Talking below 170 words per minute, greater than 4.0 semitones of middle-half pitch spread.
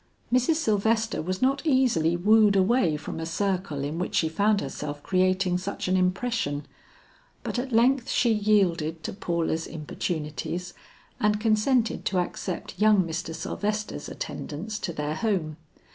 Yes: average, 145 wpm; average, 4.9 semitones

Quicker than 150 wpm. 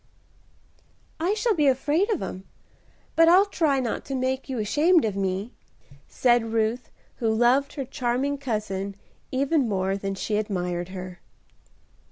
No: average, 145 wpm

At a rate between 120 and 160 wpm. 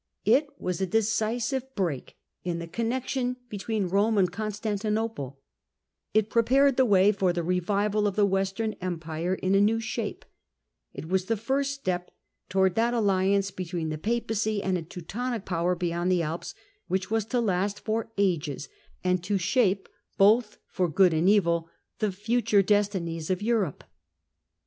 Yes: average, 155 wpm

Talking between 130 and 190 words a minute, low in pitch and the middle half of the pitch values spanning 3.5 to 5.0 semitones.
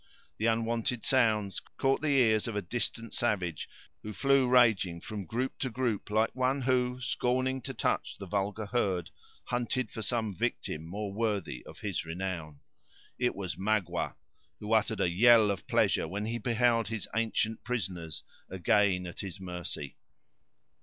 Yes: average, 155 wpm; low, 110 Hz; average, 4.3 semitones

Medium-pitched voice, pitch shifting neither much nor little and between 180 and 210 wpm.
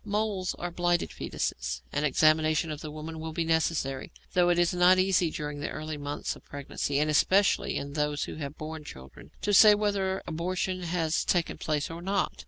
Yes: medium, 160 Hz; average, 3.4 semitones; average, 190 wpm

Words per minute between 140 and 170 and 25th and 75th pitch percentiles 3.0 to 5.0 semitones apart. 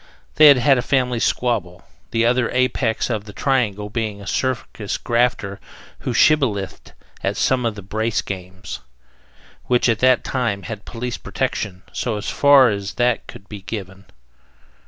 Yes: average, 155 wpm; average, 3.7 semitones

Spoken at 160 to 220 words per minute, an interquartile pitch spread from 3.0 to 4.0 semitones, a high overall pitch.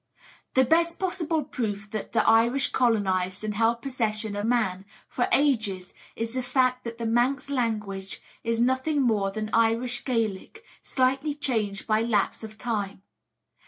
No: average, 150 wpm; average, 3.3 semitones; high, 230 Hz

